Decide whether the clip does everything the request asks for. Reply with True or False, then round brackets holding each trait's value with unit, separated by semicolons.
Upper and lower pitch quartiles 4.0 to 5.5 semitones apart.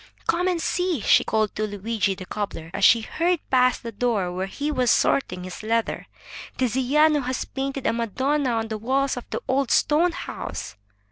True (4.5 semitones)